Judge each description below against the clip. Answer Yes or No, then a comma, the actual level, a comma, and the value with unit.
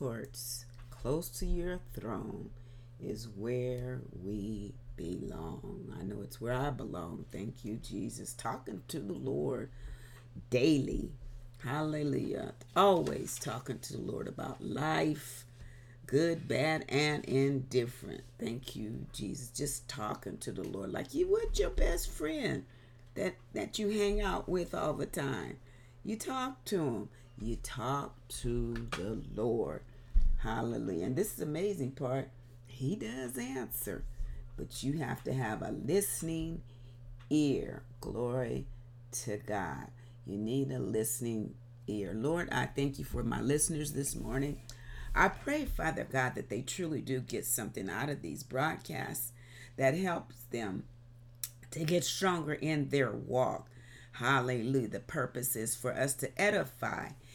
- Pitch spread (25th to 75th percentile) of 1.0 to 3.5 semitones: Yes, average, 3.2 semitones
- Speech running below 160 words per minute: Yes, average, 140 wpm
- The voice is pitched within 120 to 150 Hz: Yes, low, 125 Hz